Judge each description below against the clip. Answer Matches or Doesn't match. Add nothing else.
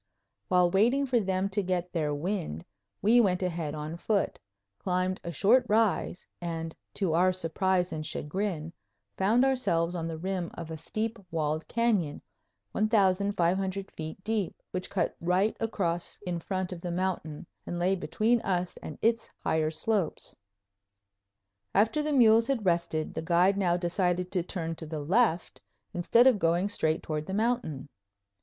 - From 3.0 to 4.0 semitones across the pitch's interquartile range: Matches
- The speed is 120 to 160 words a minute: Matches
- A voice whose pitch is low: Doesn't match